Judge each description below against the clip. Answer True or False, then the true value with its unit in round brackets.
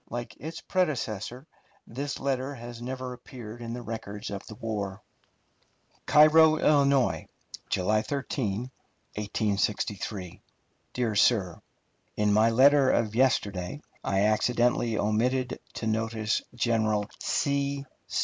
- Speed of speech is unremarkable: False (110 wpm)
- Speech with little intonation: False (3.7 semitones)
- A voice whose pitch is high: False (115 Hz)